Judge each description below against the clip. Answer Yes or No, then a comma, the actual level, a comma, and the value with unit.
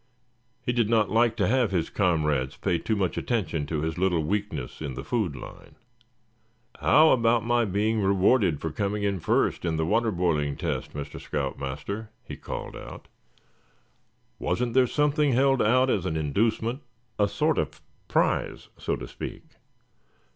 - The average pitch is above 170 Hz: No, low, 100 Hz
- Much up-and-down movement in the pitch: Yes, wide, 6.5 semitones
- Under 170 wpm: Yes, average, 160 wpm